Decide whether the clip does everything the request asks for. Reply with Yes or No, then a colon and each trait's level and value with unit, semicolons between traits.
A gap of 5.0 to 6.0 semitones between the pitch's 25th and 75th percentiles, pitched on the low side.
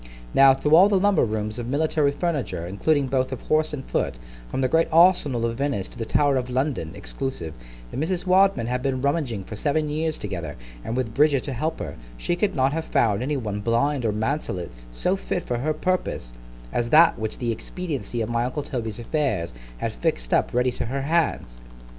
Yes: average, 5.3 semitones; low, 130 Hz